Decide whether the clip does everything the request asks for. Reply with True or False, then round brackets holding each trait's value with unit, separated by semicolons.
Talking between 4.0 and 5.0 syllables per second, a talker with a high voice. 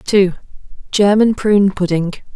True (4.5 syllables/s; 195 Hz)